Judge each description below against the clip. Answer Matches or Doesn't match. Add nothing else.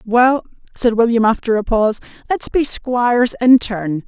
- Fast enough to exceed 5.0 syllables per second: Doesn't match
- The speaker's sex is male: Doesn't match